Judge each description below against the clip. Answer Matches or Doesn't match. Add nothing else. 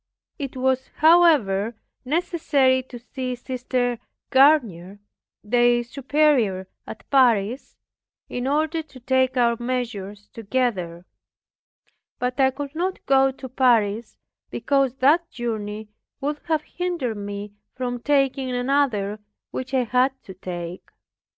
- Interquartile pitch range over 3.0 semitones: Matches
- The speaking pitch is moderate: Doesn't match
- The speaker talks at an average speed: Doesn't match